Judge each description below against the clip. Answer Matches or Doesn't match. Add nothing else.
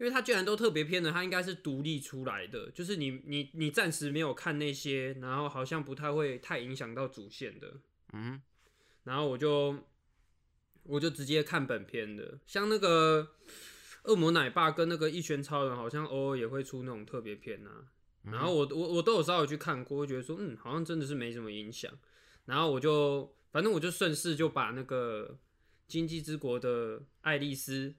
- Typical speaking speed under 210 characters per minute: Doesn't match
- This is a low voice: Doesn't match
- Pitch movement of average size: Matches